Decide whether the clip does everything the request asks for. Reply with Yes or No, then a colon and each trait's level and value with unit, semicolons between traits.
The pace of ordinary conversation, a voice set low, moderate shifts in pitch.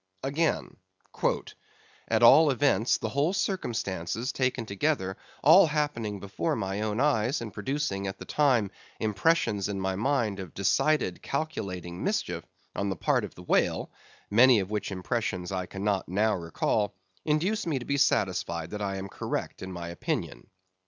No: average, 155 wpm; low, 105 Hz; wide, 6.5 semitones